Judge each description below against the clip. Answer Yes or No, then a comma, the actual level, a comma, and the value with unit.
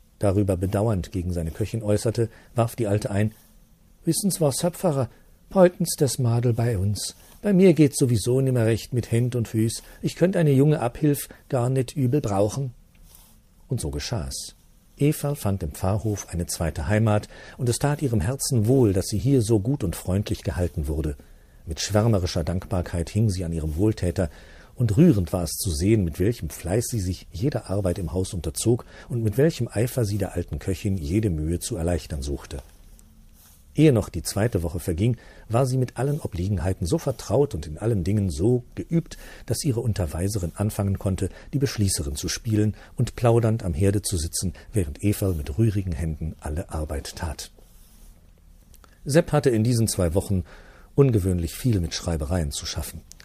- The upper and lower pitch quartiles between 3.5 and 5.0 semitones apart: No, wide, 5.5 semitones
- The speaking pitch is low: Yes, low, 105 Hz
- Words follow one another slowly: No, average, 175 wpm